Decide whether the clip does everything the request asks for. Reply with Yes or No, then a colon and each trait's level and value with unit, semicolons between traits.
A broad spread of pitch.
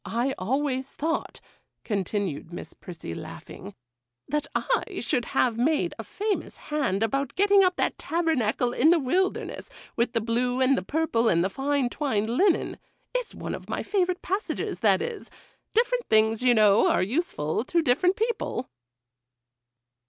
Yes: wide, 7.4 semitones